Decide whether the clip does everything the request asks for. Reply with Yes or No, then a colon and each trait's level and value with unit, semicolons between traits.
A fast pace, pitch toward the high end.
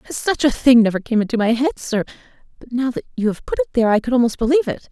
Yes: fast, 270 wpm; high, 240 Hz